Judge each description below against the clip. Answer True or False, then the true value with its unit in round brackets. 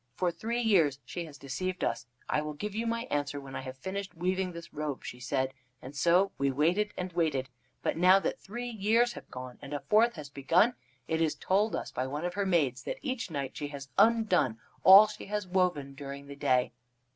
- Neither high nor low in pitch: True (170 Hz)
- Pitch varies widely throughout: True (6.2 semitones)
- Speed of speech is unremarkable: False (215 wpm)